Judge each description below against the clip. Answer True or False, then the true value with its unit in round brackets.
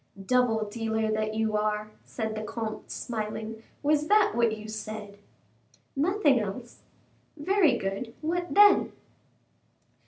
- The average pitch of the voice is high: True (220 Hz)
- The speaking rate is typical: False (120 wpm)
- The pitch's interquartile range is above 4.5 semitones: True (5.1 semitones)